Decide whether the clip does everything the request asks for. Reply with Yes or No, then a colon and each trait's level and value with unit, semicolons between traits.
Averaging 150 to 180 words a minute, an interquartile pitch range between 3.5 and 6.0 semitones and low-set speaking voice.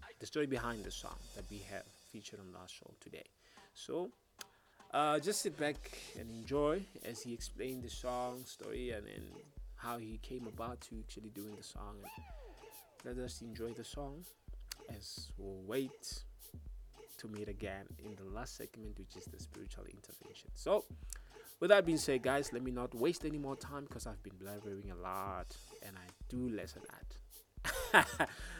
Yes: average, 170 wpm; average, 5.0 semitones; low, 115 Hz